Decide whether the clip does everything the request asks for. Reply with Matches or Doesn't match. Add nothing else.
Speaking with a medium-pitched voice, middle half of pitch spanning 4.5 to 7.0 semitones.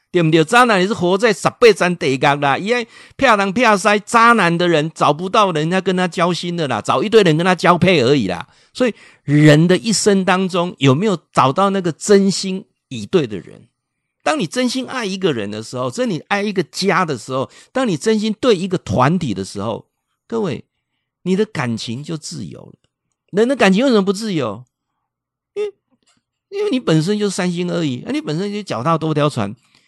Matches